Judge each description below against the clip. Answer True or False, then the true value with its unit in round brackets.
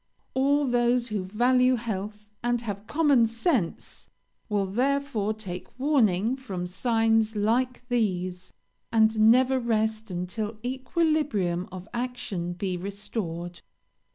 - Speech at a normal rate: False (110 wpm)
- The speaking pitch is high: True (220 Hz)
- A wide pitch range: False (4.2 semitones)